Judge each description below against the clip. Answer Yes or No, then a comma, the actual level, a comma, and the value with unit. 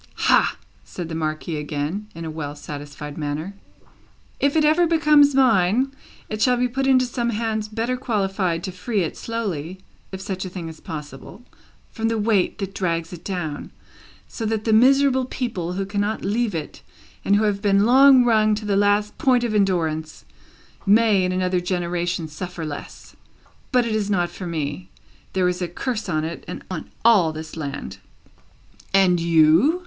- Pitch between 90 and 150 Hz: No, high, 195 Hz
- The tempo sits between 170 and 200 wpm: Yes, average, 175 wpm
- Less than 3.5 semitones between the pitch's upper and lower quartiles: No, wide, 5.4 semitones